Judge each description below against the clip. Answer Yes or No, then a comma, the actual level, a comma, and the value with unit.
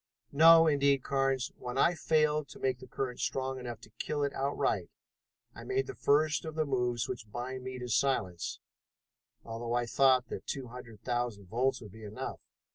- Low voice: Yes, low, 130 Hz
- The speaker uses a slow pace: No, average, 185 wpm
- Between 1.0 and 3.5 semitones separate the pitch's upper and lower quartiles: Yes, average, 2.7 semitones